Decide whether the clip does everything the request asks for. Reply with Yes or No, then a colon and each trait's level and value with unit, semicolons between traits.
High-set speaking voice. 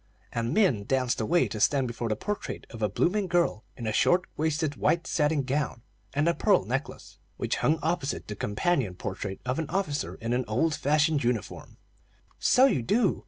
No: medium, 140 Hz